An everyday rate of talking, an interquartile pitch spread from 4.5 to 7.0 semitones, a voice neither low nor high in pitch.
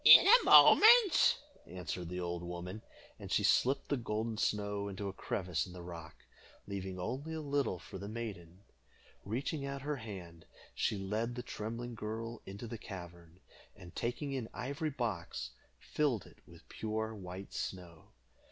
No: average, 160 wpm; average, 5.1 semitones; low, 105 Hz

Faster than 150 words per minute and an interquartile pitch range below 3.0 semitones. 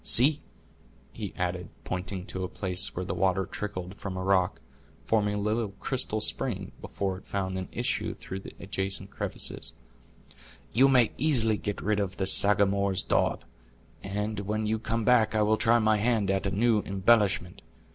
Yes: average, 170 wpm; narrow, 2.4 semitones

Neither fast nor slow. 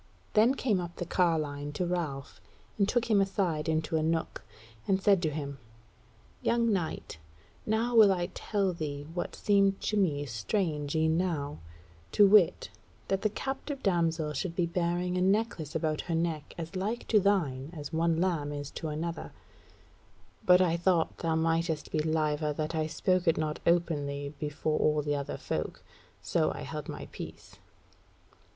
Yes: average, 165 wpm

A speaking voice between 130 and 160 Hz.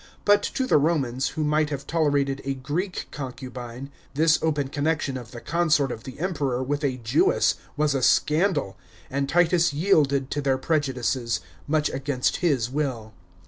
Yes: medium, 140 Hz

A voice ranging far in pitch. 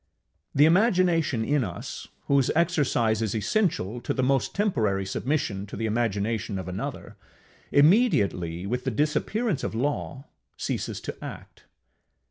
Yes: wide, 7.0 semitones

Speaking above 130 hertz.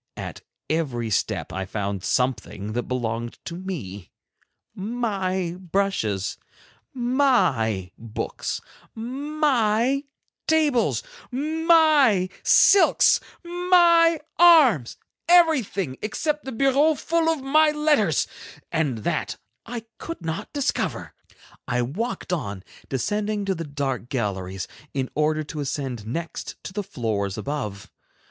Yes: high, 190 Hz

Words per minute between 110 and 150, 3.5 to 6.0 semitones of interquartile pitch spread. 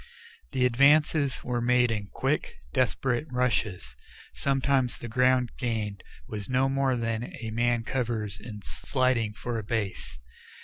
No: slow, 135 wpm; narrow, 2.6 semitones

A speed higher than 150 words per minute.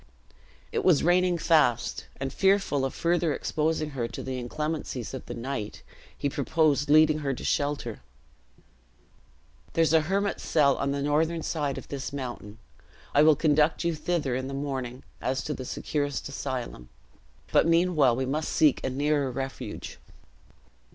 Yes: average, 160 wpm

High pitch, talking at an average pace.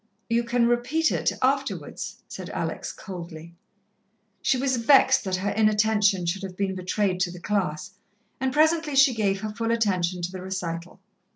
Yes: high, 210 Hz; average, 165 wpm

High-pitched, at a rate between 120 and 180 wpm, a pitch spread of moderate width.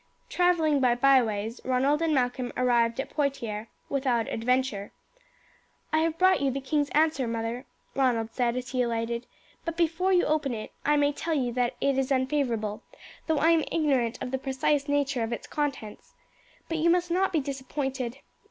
Yes: very high, 265 Hz; average, 175 wpm; average, 3.9 semitones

